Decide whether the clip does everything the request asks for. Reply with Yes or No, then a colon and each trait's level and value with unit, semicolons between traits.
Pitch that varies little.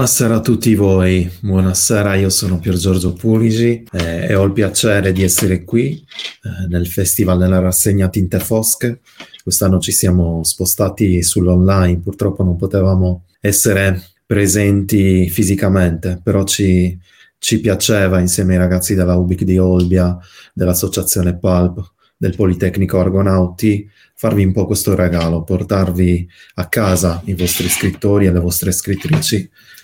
Yes: narrow, 2.1 semitones